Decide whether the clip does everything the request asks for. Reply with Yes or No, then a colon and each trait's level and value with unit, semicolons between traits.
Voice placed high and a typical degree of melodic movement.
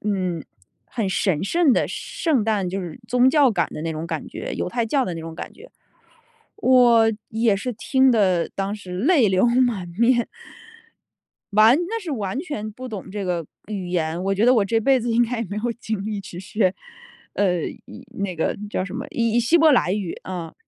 Yes: high, 215 Hz; average, 4.8 semitones